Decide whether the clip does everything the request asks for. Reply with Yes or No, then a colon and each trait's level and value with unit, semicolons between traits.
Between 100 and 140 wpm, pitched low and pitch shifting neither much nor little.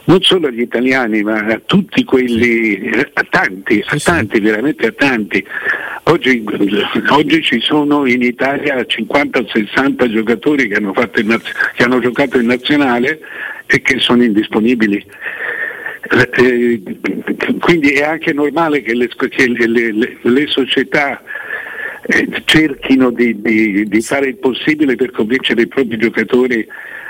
Yes: average, 130 wpm; low, 130 Hz; average, 3.8 semitones